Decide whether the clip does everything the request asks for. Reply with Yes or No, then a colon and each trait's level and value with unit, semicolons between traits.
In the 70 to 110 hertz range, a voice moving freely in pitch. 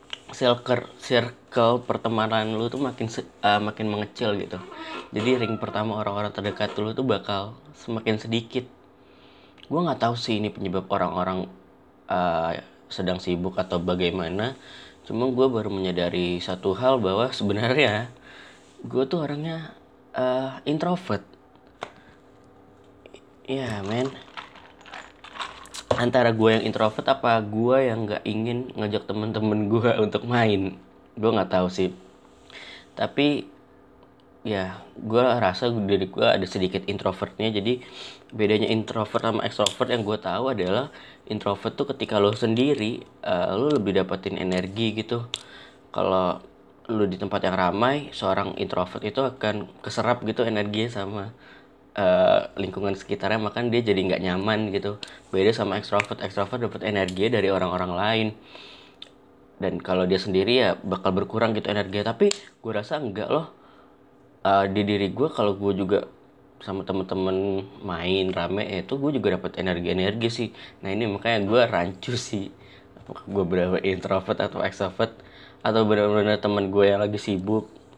No: low, 105 Hz; average, 3.0 semitones